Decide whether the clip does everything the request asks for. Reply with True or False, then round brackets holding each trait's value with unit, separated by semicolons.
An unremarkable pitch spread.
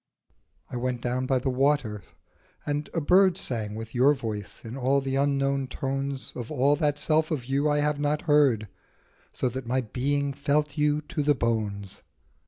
True (3.0 semitones)